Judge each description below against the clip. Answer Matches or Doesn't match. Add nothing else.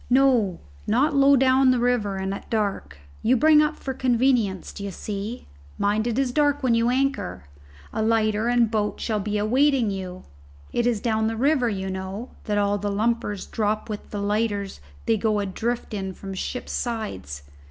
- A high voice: Matches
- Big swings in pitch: Doesn't match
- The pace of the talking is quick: Doesn't match